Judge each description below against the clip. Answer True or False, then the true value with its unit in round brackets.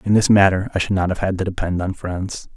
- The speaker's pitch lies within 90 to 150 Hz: True (95 Hz)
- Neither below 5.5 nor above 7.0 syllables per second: True (5.9 syllables/s)